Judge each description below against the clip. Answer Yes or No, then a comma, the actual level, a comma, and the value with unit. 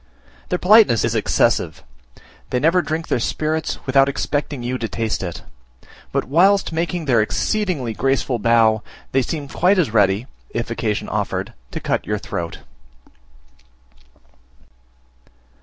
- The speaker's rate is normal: No, slow, 130 wpm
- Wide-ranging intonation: Yes, wide, 6.2 semitones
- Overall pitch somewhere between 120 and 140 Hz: Yes, low, 135 Hz